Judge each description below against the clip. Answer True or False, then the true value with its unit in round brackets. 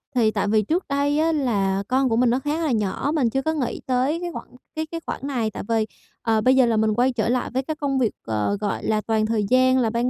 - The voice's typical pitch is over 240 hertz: True (250 Hz)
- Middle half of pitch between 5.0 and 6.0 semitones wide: False (4.3 semitones)